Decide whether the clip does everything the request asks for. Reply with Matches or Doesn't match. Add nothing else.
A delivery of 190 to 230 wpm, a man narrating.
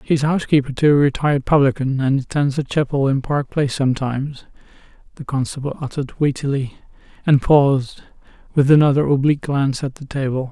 Doesn't match